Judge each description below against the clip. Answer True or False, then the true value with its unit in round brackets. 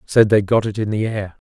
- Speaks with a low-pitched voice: True (105 Hz)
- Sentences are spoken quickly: True (285 wpm)